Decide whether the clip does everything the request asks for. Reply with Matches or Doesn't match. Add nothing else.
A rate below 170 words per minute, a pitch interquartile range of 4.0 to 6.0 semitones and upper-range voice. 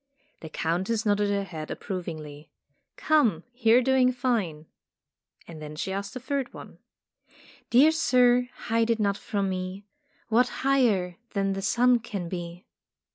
Matches